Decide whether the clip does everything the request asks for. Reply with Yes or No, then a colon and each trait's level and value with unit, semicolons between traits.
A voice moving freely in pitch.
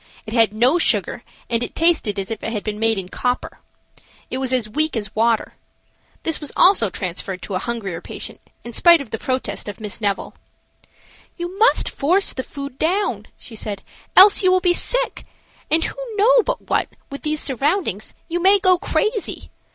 Yes: wide, 8.4 semitones